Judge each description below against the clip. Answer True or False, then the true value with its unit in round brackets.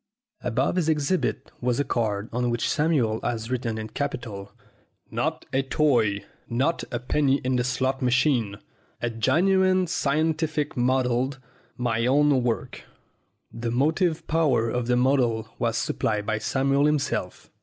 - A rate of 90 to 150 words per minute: True (140 wpm)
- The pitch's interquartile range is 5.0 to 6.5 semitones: False (4.0 semitones)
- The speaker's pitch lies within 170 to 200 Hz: False (125 Hz)